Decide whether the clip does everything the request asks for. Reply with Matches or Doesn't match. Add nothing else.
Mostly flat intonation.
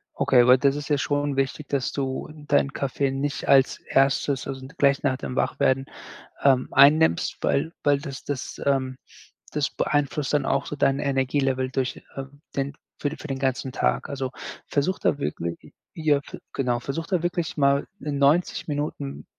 Matches